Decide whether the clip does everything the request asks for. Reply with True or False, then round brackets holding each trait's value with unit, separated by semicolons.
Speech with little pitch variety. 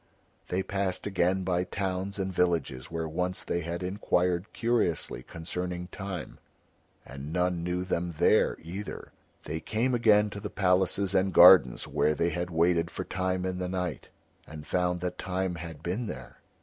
True (2.0 semitones)